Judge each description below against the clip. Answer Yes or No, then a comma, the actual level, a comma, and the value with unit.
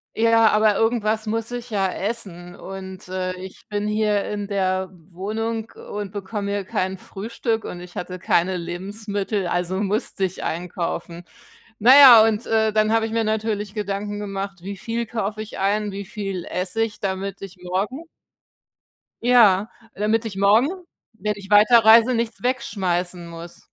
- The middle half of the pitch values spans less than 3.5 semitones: Yes, average, 2.8 semitones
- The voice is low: No, high, 205 Hz